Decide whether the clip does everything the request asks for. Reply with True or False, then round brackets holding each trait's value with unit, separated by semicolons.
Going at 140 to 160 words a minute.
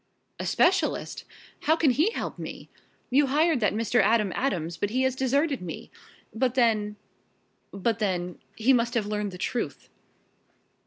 True (155 wpm)